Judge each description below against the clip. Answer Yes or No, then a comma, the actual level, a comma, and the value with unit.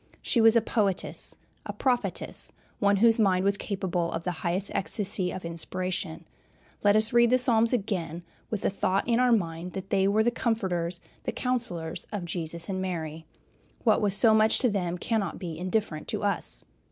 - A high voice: Yes, high, 195 Hz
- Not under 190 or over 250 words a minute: No, average, 180 wpm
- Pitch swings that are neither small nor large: Yes, average, 4.2 semitones